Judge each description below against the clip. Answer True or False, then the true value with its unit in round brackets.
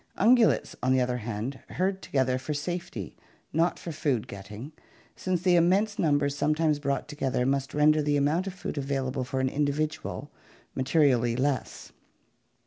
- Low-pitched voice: False (145 Hz)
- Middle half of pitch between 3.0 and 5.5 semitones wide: True (3.8 semitones)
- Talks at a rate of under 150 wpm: False (160 wpm)